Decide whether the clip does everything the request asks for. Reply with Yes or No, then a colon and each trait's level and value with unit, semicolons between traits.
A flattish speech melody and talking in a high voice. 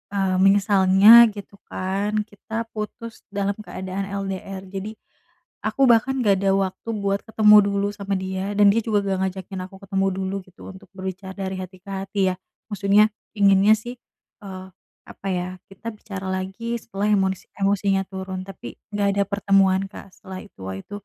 Yes: narrow, 1.4 semitones; high, 195 Hz